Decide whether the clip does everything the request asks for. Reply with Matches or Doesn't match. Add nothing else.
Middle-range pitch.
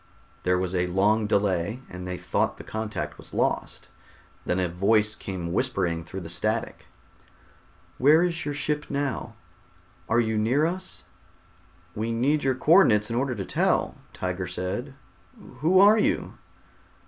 Doesn't match